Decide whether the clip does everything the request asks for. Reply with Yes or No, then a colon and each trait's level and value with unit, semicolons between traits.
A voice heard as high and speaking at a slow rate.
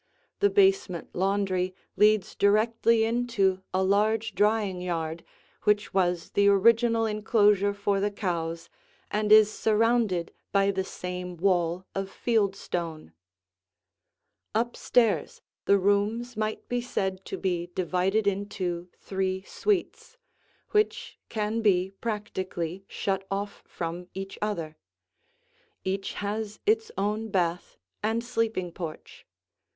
Yes: high, 200 Hz; slow, 115 wpm